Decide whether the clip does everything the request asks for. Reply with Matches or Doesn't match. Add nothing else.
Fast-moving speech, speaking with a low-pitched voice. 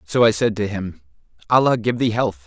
Matches